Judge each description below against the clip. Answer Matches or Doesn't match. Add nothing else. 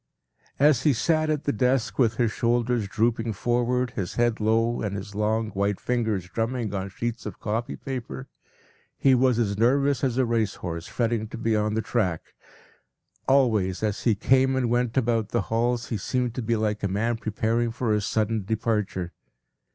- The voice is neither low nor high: Doesn't match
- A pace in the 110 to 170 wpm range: Doesn't match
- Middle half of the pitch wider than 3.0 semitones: Doesn't match